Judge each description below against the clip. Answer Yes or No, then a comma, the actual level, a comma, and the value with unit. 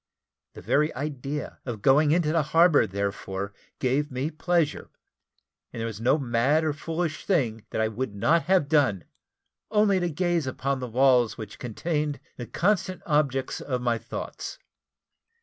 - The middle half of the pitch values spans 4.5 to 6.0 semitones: Yes, average, 4.8 semitones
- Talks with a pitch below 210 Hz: Yes, medium, 140 Hz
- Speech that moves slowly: No, average, 155 wpm